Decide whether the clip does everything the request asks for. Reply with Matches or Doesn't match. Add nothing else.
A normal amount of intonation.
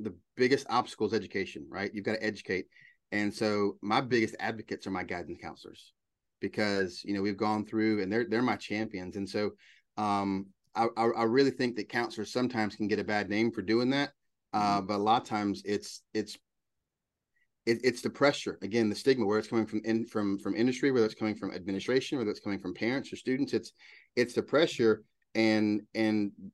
Doesn't match